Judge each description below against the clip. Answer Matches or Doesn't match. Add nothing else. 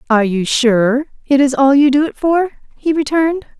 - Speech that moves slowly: Doesn't match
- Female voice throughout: Matches